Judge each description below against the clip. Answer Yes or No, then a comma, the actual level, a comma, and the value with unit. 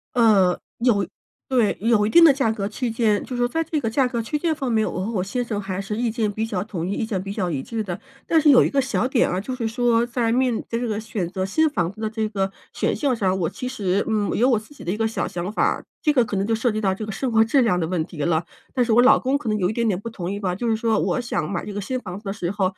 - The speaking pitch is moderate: No, high, 220 Hz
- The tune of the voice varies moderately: Yes, average, 3.7 semitones